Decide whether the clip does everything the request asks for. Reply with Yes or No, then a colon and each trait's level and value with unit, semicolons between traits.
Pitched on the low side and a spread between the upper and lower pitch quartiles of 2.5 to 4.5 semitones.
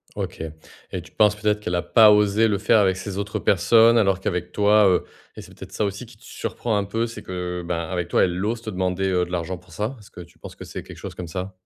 Yes: low, 100 Hz; average, 2.8 semitones